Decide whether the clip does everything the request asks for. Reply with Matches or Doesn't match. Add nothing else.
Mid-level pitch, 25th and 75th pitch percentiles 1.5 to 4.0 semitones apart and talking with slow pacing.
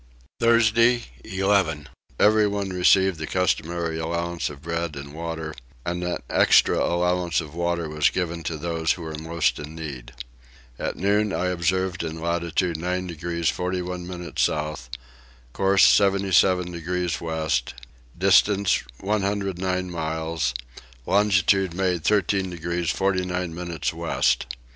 Doesn't match